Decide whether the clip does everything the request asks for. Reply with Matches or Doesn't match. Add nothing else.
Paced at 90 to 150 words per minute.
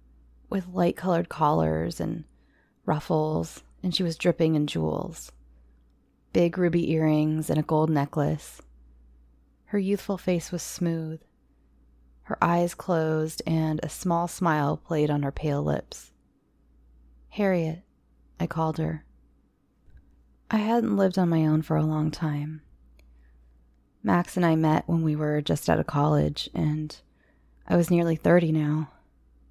Matches